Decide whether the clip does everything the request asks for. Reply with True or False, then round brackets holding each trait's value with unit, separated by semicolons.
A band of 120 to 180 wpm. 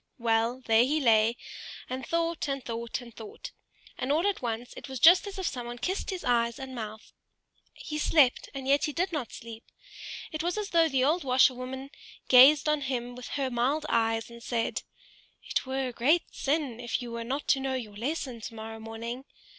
False (190 wpm)